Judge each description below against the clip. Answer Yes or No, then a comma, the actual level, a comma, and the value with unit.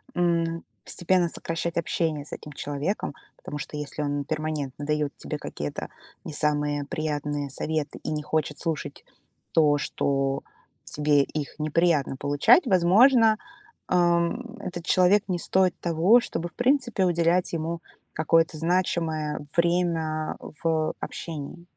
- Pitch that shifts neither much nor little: Yes, average, 3.0 semitones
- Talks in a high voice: No, medium, 160 Hz